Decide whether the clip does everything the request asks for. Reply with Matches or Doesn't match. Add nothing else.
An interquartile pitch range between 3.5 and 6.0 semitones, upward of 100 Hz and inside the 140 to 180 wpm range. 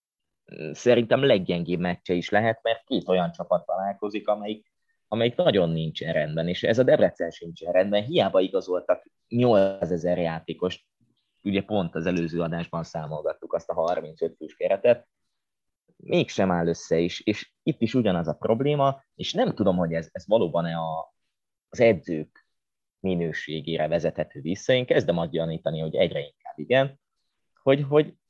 Doesn't match